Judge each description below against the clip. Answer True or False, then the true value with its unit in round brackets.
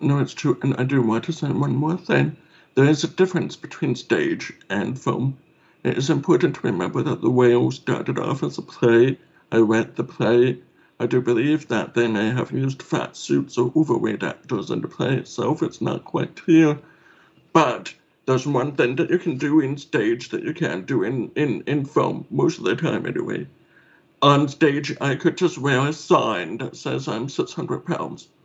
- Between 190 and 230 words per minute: True (200 wpm)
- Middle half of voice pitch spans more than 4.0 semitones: True (4.4 semitones)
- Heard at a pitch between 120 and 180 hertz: True (140 Hz)